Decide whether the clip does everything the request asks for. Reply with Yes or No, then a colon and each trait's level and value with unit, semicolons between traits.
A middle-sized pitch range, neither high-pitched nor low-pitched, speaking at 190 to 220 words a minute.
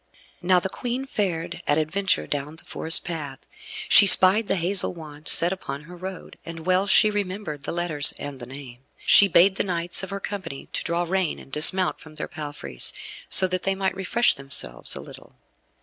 Yes: average, 4.2 semitones; medium, 175 Hz; average, 195 wpm